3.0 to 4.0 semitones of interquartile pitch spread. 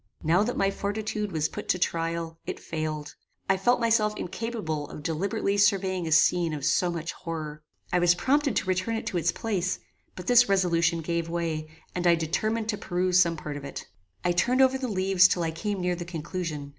Yes: average, 3.6 semitones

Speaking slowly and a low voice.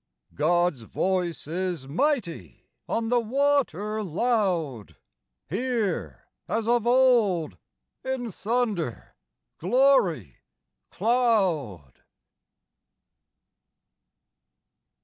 No: slow, 65 wpm; high, 200 Hz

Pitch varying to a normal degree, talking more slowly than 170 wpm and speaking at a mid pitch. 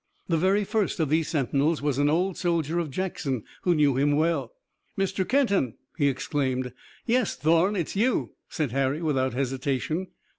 Yes: average, 5.0 semitones; average, 160 wpm; medium, 155 Hz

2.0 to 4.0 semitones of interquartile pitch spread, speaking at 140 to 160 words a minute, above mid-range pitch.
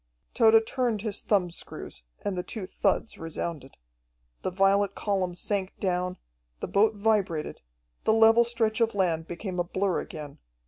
Yes: average, 3.6 semitones; average, 145 wpm; high, 195 Hz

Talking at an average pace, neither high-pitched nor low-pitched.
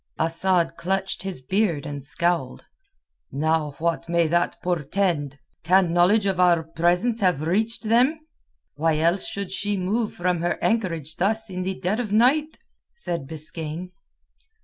Yes: average, 145 wpm; medium, 180 Hz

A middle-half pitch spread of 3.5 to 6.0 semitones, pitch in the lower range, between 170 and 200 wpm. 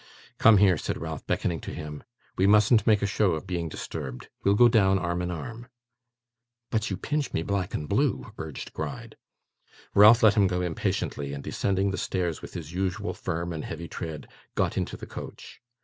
Yes: average, 3.9 semitones; very low, 95 Hz; average, 190 wpm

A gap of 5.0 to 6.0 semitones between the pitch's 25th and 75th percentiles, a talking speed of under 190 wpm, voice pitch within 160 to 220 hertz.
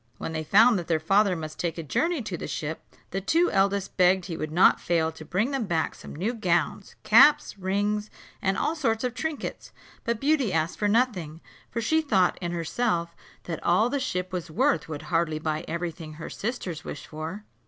No: average, 5.3 semitones; fast, 205 wpm; medium, 185 Hz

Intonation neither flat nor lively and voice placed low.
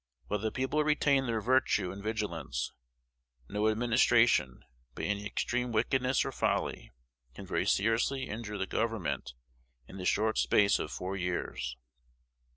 Yes: average, 3.9 semitones; low, 110 Hz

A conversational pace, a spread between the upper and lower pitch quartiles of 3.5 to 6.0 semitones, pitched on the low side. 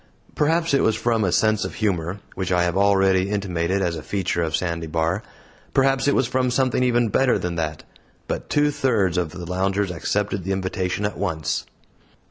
Yes: average, 190 wpm; average, 4.7 semitones; very low, 95 Hz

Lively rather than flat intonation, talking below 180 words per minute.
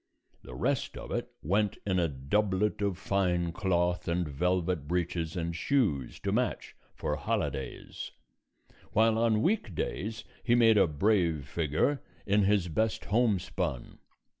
No: average, 4.1 semitones; average, 140 wpm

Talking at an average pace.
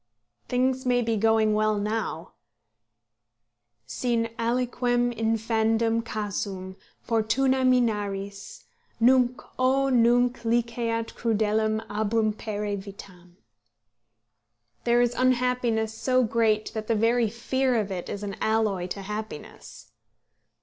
No: slow, 100 wpm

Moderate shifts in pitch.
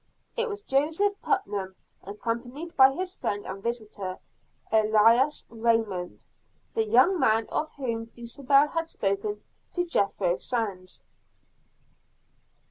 No: wide, 6.2 semitones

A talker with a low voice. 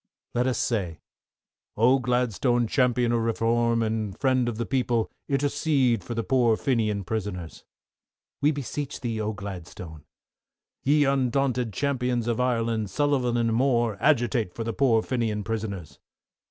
Yes: low, 120 Hz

